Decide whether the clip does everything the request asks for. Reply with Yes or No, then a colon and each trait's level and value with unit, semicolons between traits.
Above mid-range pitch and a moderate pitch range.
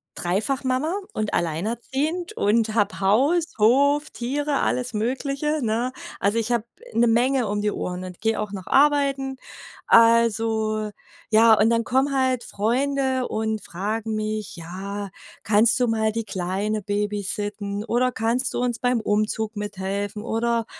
Yes: high, 225 Hz; average, 3.5 semitones